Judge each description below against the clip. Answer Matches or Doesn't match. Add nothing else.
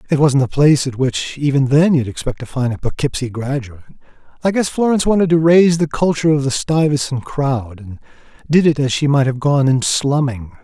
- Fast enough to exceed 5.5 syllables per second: Matches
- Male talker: Matches